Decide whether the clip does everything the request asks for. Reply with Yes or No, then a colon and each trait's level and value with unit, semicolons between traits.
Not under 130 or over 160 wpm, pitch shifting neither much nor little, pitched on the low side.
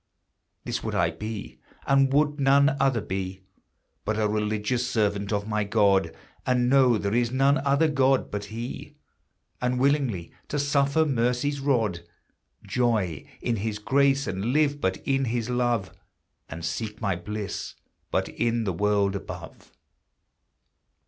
Yes: average, 140 wpm; average, 4.7 semitones; low, 115 Hz